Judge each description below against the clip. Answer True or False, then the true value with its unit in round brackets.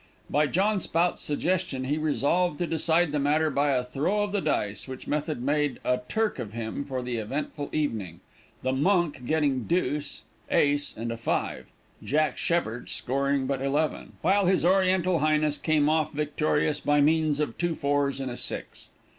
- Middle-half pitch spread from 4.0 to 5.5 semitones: False (3.3 semitones)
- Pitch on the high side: False (150 Hz)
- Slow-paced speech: False (170 wpm)